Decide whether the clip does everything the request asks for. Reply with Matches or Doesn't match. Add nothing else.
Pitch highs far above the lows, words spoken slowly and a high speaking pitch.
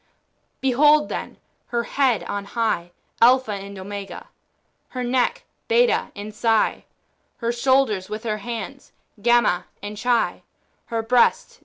Doesn't match